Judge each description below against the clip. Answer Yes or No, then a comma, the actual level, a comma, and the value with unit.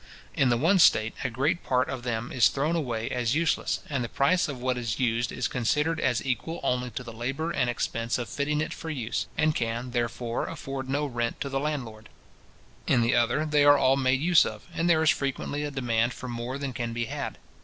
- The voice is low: Yes, low, 130 Hz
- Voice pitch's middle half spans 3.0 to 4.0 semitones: Yes, average, 3.6 semitones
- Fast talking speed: Yes, fast, 225 wpm